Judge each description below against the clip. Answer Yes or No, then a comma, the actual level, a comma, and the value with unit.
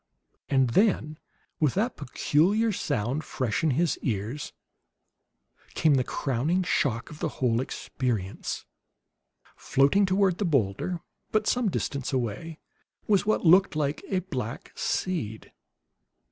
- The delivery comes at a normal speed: No, slow, 120 wpm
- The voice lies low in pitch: No, medium, 150 Hz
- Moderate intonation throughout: No, wide, 6.7 semitones